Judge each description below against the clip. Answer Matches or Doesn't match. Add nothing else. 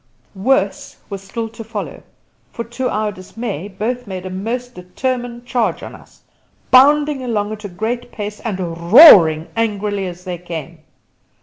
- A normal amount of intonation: Matches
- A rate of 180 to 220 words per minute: Doesn't match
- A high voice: Matches